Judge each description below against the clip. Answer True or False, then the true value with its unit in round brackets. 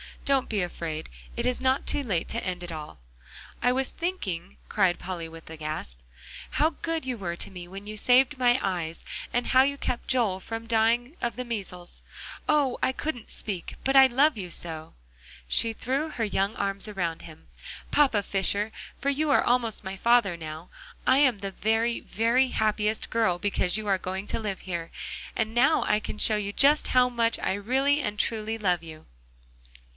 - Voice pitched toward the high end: True (215 Hz)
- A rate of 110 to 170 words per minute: False (190 wpm)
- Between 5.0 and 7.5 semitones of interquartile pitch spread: True (5.4 semitones)